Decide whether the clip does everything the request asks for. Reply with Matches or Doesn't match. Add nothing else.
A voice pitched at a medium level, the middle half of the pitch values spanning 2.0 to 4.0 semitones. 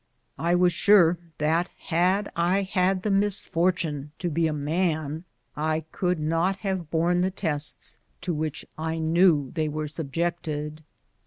Matches